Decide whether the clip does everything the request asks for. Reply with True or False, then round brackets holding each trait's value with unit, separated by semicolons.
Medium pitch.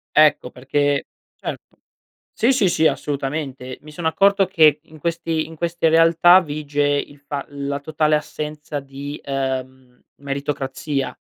True (145 Hz)